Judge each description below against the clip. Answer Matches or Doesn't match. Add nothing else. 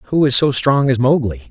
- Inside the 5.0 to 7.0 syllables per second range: Doesn't match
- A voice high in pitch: Doesn't match